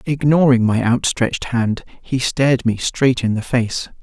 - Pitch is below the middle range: Yes, low, 125 Hz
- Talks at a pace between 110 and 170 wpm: Yes, average, 165 wpm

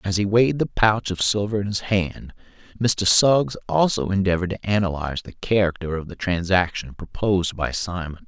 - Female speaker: No, male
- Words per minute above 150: Yes, average, 175 wpm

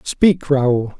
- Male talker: Yes, male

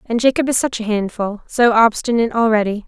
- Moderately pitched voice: No, high, 225 Hz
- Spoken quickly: No, average, 190 wpm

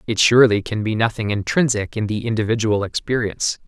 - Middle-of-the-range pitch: No, low, 110 Hz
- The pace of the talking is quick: No, average, 165 wpm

